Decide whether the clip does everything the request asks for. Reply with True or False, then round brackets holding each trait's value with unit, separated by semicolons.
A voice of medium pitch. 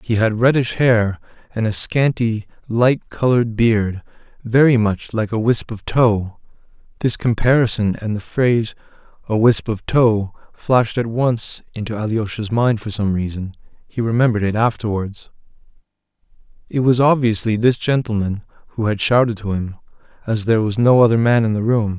False (110 Hz)